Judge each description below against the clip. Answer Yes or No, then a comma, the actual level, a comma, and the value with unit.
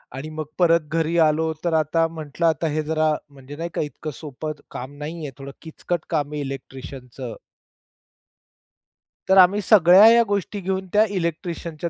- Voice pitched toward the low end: No, medium, 160 Hz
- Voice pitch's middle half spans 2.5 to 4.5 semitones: Yes, average, 2.8 semitones